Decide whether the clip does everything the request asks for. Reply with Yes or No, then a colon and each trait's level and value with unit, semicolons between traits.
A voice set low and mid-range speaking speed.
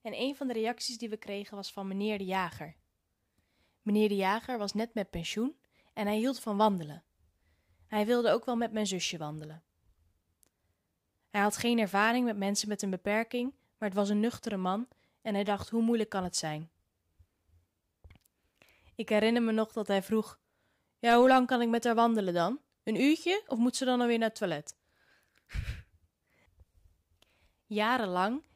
No: high, 205 Hz; average, 175 wpm